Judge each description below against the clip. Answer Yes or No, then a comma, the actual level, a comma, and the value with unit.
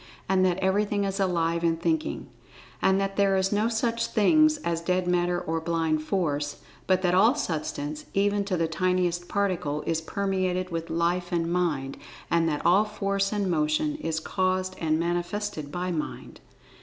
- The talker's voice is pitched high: No, medium, 180 Hz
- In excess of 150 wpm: Yes, average, 170 wpm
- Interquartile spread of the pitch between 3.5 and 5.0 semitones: No, average, 3.1 semitones